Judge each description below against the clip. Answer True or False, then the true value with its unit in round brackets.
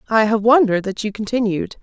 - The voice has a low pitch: False (215 Hz)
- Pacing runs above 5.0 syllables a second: True (6.2 syllables/s)